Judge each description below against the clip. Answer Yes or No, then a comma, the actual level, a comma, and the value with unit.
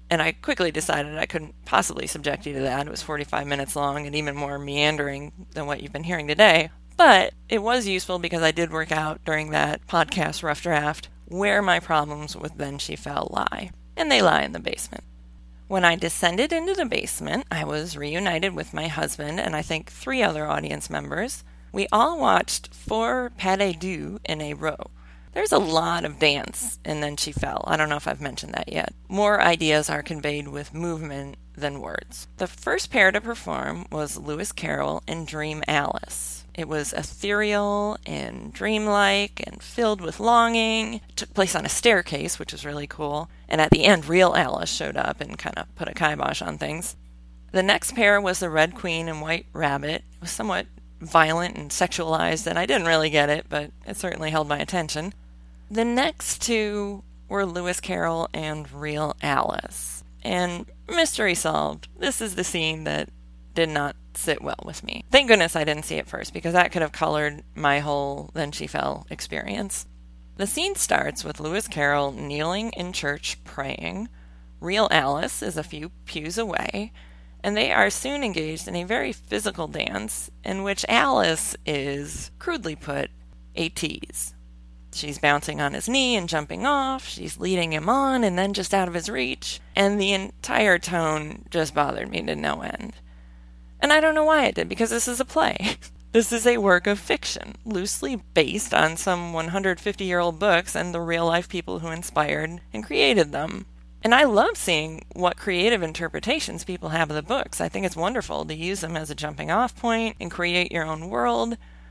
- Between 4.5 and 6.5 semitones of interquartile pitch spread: Yes, average, 5.2 semitones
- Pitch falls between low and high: Yes, medium, 160 Hz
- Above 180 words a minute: Yes, average, 190 wpm